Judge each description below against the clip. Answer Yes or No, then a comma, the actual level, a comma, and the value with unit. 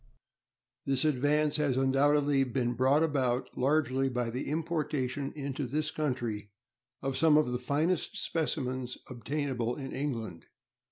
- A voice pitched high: No, low, 135 Hz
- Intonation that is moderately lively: Yes, average, 3.0 semitones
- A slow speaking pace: Yes, slow, 125 wpm